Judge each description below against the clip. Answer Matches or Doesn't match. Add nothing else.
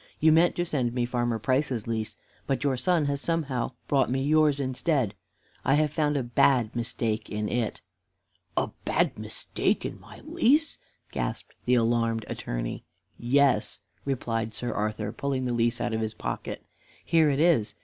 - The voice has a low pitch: Matches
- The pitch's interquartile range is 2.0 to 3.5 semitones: Doesn't match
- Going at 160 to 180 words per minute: Matches